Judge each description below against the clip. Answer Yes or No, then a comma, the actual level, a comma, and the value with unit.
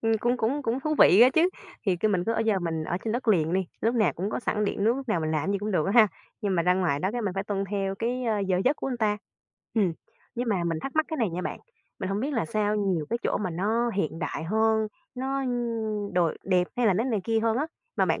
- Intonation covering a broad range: No, average, 4.3 semitones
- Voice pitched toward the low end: No, high, 210 Hz